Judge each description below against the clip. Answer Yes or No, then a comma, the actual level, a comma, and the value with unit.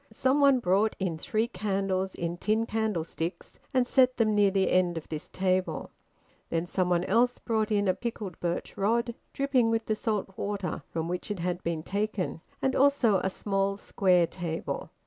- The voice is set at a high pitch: Yes, high, 200 Hz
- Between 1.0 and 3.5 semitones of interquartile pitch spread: No, average, 3.9 semitones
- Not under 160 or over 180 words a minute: Yes, average, 175 wpm